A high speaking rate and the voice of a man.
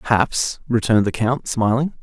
No: average, 150 wpm; male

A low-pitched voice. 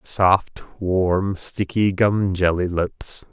Yes: very low, 95 Hz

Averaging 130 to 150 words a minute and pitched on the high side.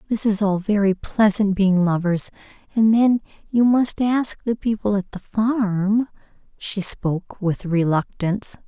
Yes: average, 140 wpm; high, 205 Hz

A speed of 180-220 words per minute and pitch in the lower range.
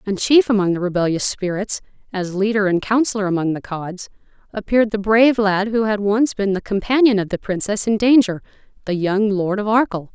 No: average, 195 wpm; high, 205 Hz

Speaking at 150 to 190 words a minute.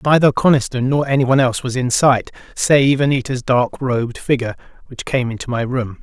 Yes: average, 180 wpm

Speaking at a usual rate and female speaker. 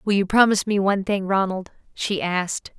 Yes: average, 195 wpm; female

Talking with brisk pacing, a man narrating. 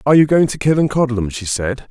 Yes: fast, 220 wpm; male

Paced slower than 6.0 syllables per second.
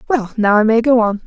No: 6.1 syllables/s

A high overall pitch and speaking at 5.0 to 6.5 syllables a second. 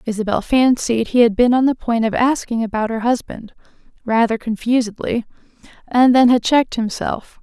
Yes: high, 235 Hz; 5.1 syllables/s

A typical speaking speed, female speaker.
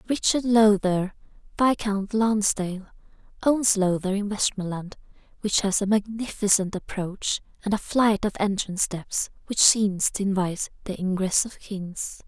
No: slow, 130 wpm; female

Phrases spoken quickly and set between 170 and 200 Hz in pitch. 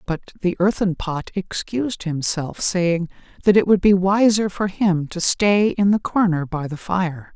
No: average, 180 wpm; medium, 185 Hz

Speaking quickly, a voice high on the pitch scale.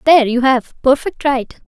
No: average, 180 wpm; very high, 265 Hz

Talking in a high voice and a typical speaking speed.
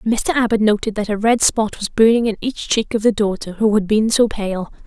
No: high, 215 Hz; fast, 245 wpm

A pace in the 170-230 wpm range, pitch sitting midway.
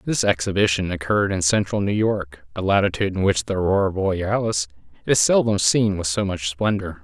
No: average, 180 wpm; very low, 95 Hz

